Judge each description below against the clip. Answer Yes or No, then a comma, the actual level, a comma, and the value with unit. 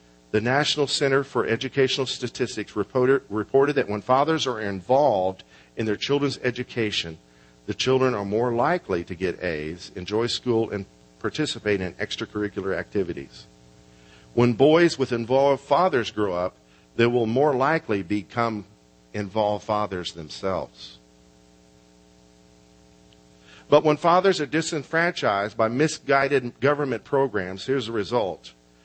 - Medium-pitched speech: No, low, 110 Hz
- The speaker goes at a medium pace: No, slow, 120 wpm